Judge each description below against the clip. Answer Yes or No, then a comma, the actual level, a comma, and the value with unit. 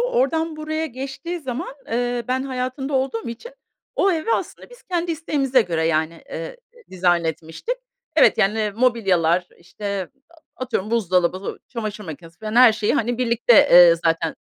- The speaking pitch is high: Yes, high, 235 Hz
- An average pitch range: No, wide, 7.1 semitones